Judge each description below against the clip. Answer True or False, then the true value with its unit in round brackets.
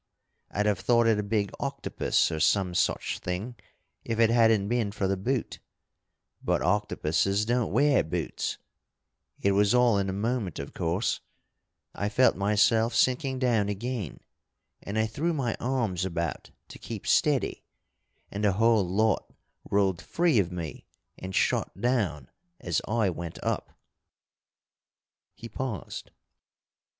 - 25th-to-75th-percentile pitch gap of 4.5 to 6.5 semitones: False (3.7 semitones)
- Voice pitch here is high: False (105 Hz)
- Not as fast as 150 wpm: True (140 wpm)